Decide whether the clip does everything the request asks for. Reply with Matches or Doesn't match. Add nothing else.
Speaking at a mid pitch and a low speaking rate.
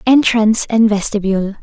Doesn't match